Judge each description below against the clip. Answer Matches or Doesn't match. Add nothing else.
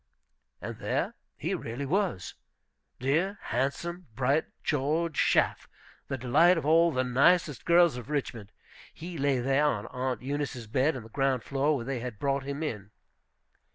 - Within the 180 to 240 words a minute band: Doesn't match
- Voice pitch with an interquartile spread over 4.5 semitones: Doesn't match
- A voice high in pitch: Doesn't match